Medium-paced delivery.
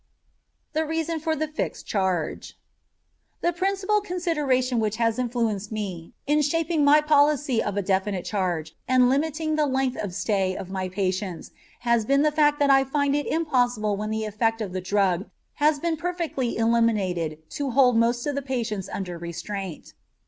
Yes: average, 170 wpm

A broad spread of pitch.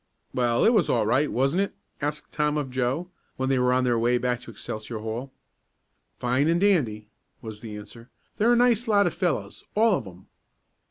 Yes: wide, 6.4 semitones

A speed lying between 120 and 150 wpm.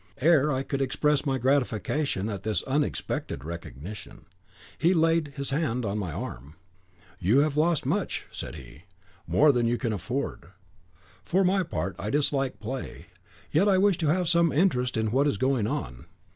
No: average, 170 wpm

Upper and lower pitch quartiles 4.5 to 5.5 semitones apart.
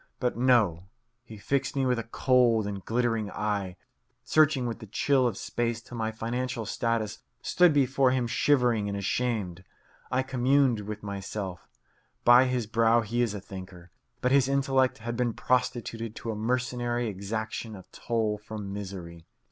No: average, 3.3 semitones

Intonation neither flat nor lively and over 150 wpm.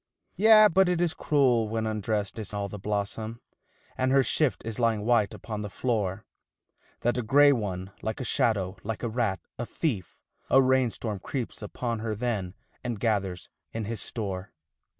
Yes: average, 3.4 semitones; average, 175 wpm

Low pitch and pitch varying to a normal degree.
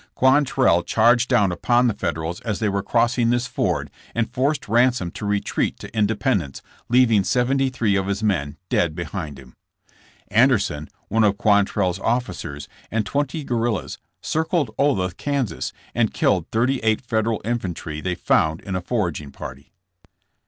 Yes: low, 110 Hz; average, 5.0 semitones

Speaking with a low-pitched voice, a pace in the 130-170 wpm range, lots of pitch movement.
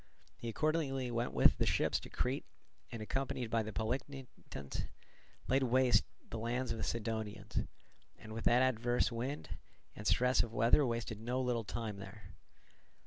No: low, 120 Hz; average, 155 wpm; average, 2.7 semitones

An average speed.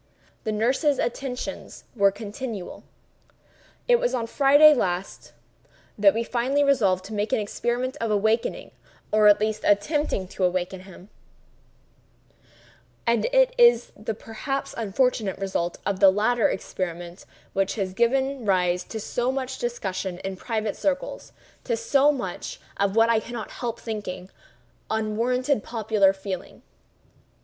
No: slow, 125 wpm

